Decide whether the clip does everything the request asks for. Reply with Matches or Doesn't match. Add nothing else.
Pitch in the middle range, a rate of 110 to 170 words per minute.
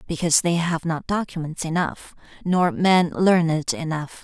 Matches